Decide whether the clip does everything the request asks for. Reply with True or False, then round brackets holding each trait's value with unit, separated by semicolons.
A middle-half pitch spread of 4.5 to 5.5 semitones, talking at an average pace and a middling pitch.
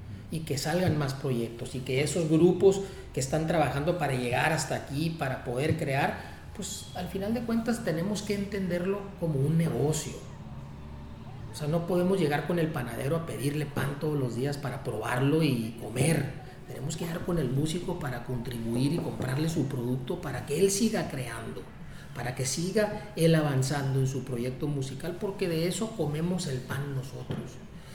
True (5.0 semitones; 175 wpm; 145 Hz)